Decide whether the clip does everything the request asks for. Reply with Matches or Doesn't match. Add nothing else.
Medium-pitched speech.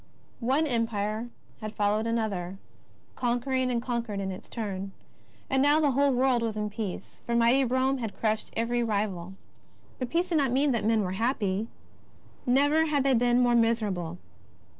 Doesn't match